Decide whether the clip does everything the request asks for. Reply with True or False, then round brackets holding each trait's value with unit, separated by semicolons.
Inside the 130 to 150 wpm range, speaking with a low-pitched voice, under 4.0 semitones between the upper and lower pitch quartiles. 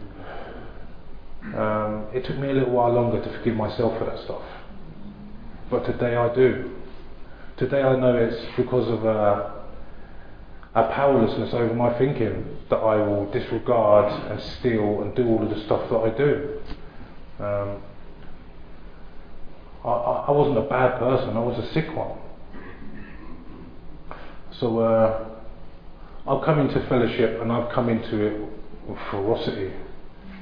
True (140 wpm; 110 Hz; 3.6 semitones)